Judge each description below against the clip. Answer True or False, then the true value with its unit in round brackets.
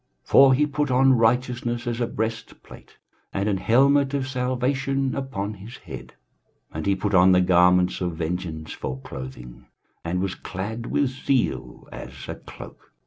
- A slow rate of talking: False (160 wpm)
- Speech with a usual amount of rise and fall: False (6.5 semitones)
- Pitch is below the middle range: True (110 Hz)